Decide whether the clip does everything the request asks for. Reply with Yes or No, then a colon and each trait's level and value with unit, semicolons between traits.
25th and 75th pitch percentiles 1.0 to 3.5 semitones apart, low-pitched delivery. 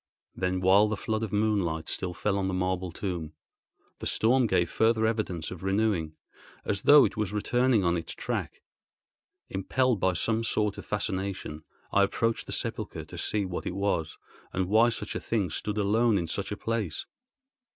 Yes: average, 3.2 semitones; low, 100 Hz